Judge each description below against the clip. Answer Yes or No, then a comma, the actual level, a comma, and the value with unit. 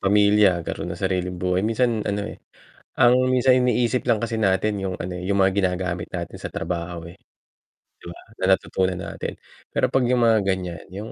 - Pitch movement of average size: Yes, average, 3.8 semitones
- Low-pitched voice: Yes, very low, 95 Hz